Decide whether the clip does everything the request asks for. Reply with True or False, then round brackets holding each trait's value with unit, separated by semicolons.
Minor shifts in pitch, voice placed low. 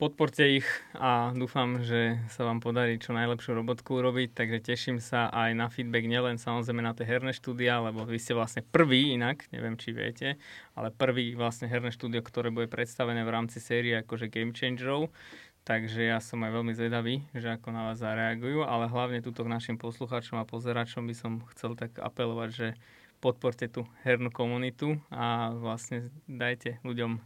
True (1.3 semitones; 120 Hz)